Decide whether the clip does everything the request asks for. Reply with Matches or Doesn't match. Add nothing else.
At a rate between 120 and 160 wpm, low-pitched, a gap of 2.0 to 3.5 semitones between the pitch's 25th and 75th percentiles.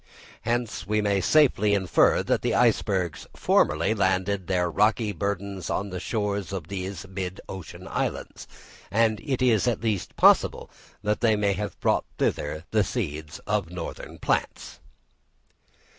Matches